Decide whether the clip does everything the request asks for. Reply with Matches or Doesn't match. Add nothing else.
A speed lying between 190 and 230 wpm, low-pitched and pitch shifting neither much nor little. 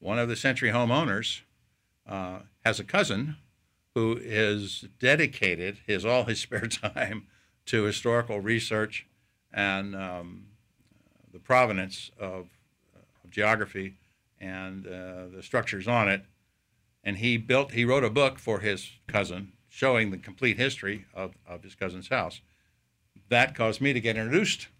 Doesn't match